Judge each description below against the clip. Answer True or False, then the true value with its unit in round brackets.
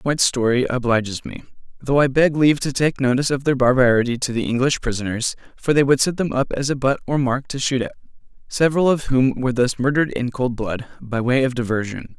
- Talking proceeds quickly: True (220 wpm)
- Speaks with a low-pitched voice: True (130 Hz)